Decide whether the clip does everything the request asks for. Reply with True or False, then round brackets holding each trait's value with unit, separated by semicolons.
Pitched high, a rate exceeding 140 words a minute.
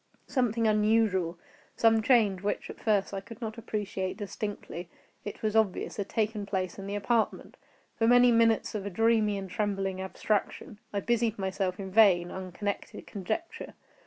True (205 Hz; 150 wpm)